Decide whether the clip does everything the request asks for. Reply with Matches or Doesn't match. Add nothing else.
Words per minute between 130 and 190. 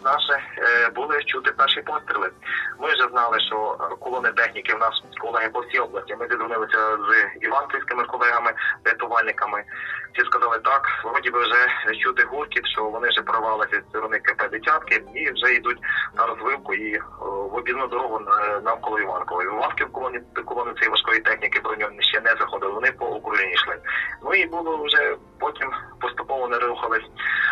Matches